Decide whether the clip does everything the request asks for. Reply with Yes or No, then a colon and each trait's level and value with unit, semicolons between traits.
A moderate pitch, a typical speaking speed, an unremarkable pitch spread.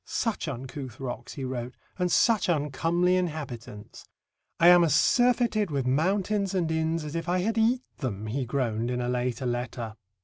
No: medium, 150 Hz; average, 170 wpm; wide, 6.4 semitones